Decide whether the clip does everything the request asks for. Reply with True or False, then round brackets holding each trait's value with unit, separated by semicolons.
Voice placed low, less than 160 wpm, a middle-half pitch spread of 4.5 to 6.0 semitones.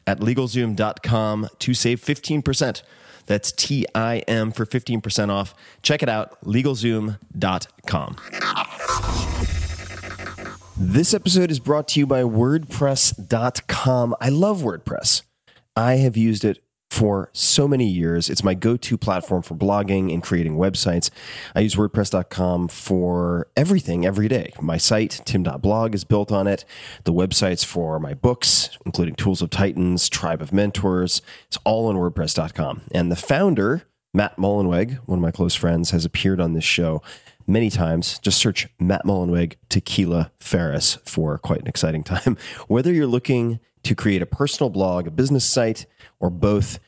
True (100 Hz; 150 wpm; 5.2 semitones)